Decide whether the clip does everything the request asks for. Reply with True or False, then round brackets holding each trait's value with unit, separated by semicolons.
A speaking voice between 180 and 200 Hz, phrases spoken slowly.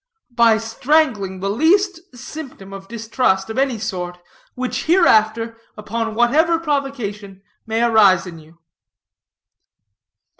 False (225 Hz; 110 wpm)